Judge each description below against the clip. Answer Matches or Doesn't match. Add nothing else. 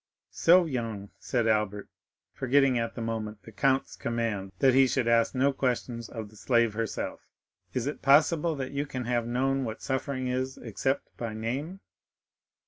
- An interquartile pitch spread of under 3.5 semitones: Matches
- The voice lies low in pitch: Matches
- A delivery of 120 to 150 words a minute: Doesn't match